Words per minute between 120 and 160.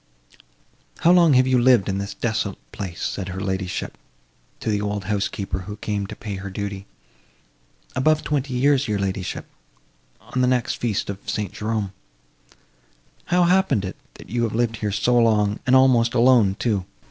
No: average, 170 wpm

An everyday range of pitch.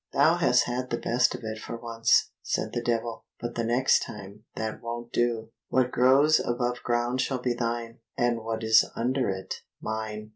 No: narrow, 1.5 semitones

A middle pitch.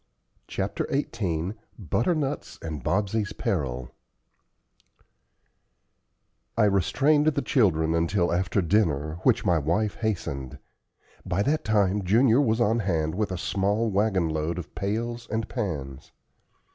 No: low, 100 Hz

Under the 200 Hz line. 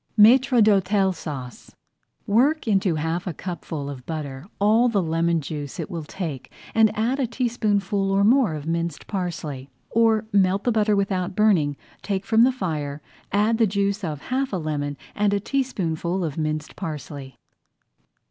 Yes: high, 190 Hz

